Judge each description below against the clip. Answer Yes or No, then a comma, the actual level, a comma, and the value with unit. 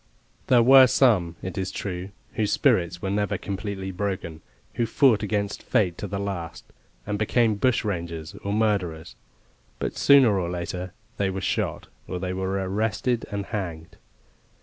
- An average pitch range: Yes, average, 3.0 semitones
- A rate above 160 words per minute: No, average, 150 wpm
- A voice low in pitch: Yes, low, 100 Hz